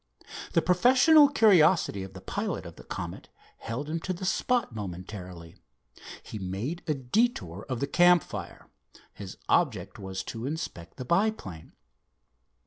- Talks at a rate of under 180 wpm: Yes, slow, 135 wpm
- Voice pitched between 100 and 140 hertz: Yes, low, 135 Hz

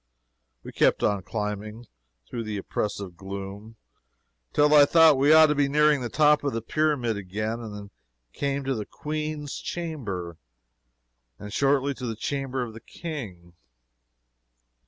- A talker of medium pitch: No, low, 125 Hz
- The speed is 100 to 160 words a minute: Yes, average, 150 wpm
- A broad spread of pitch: Yes, wide, 6.0 semitones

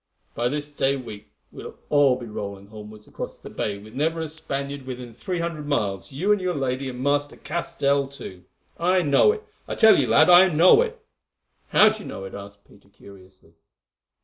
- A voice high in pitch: No, medium, 140 Hz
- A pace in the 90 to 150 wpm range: No, average, 200 wpm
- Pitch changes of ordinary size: No, wide, 7.6 semitones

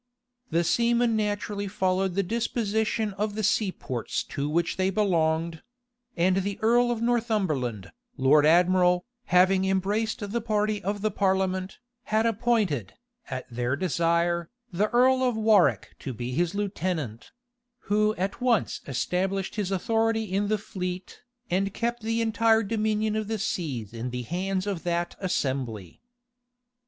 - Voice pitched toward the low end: No, high, 195 Hz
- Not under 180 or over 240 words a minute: No, average, 145 wpm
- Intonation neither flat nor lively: Yes, average, 4.0 semitones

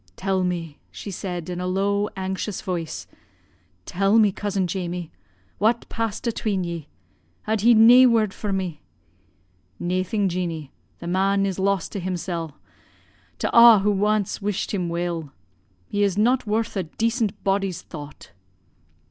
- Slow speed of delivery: No, average, 145 wpm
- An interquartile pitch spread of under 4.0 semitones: Yes, average, 3.0 semitones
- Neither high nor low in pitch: No, high, 195 Hz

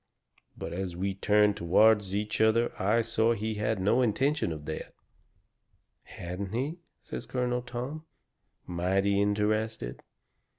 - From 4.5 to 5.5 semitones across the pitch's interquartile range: No, average, 3.2 semitones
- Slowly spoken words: Yes, slow, 130 wpm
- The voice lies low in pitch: Yes, low, 105 Hz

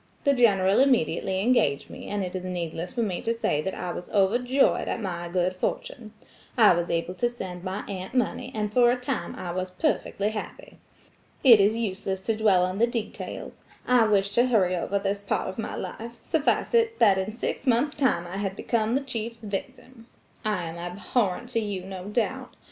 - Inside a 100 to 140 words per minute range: No, average, 195 wpm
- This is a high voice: Yes, high, 205 Hz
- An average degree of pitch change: Yes, average, 4.2 semitones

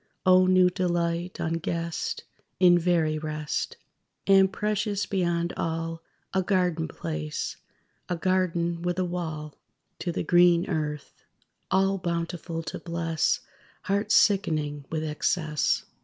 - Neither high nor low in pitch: Yes, medium, 170 Hz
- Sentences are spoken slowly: Yes, slow, 115 wpm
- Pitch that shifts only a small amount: Yes, narrow, 2.3 semitones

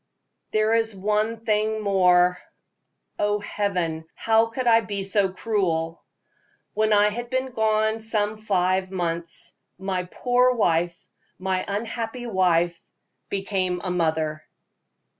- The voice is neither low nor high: No, high, 205 Hz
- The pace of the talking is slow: Yes, slow, 120 wpm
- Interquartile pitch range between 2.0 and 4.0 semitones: Yes, average, 3.5 semitones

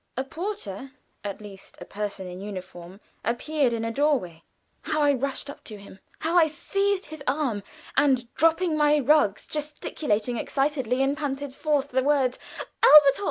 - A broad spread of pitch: Yes, wide, 5.7 semitones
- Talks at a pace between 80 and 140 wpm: No, average, 160 wpm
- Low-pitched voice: No, very high, 270 Hz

